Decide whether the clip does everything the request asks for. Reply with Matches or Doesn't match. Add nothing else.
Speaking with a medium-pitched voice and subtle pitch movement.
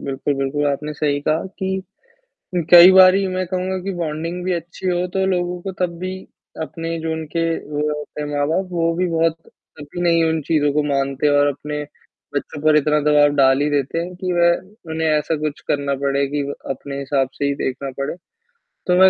Doesn't match